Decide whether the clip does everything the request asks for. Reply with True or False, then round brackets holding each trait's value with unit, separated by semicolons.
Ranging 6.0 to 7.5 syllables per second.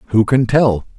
False (3.5 syllables/s)